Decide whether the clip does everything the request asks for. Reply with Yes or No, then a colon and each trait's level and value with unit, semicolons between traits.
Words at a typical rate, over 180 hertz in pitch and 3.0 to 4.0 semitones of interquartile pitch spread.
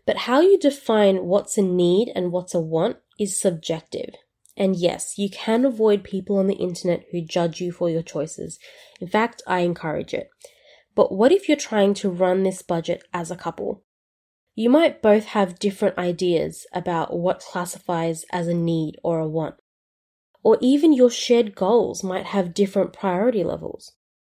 Yes: average, 175 wpm; high, 190 Hz; average, 3.7 semitones